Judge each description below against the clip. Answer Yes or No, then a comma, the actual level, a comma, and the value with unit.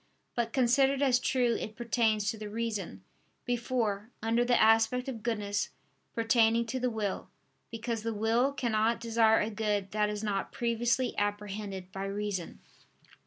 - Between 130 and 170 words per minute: Yes, average, 150 wpm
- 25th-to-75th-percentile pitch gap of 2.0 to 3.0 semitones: Yes, narrow, 2.4 semitones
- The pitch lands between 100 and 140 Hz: No, high, 225 Hz